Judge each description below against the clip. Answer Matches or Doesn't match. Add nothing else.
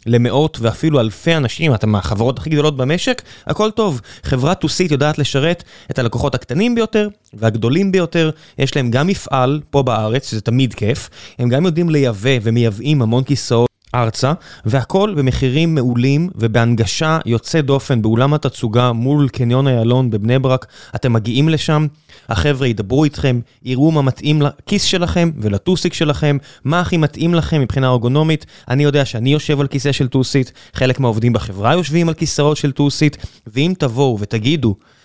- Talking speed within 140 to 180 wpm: Matches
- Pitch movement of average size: Matches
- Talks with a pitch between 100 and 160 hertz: Matches